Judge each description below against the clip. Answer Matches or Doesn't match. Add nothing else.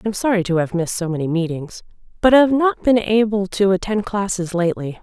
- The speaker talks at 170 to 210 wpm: Matches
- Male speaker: Doesn't match